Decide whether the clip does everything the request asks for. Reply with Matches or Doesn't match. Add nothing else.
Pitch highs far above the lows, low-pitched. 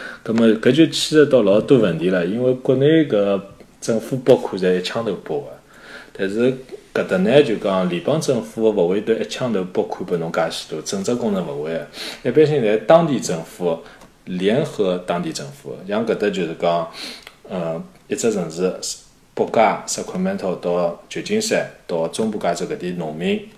Matches